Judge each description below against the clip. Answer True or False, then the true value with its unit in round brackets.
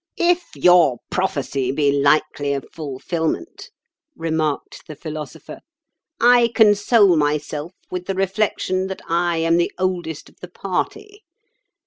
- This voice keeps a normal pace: False (120 wpm)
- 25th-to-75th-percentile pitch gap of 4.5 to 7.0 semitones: False (4.1 semitones)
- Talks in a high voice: False (170 Hz)